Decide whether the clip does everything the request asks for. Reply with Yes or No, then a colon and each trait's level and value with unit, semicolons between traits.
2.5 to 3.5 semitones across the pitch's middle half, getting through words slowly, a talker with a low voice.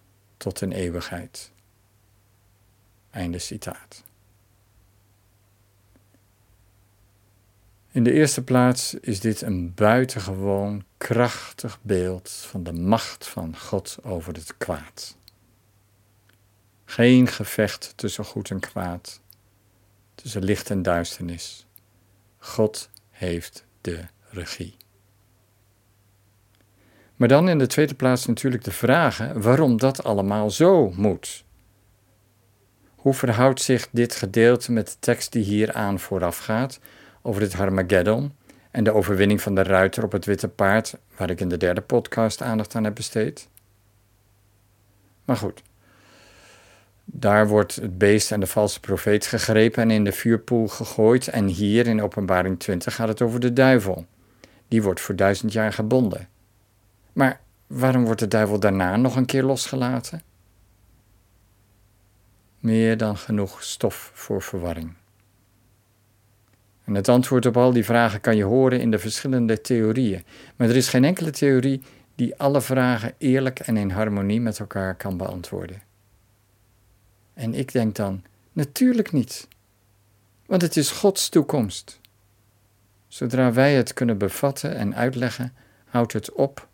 Yes: average, 3.1 semitones; slow, 130 wpm; low, 105 Hz